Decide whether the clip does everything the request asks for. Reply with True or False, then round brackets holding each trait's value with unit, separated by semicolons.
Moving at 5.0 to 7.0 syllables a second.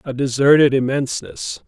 True (5.2 syllables/s)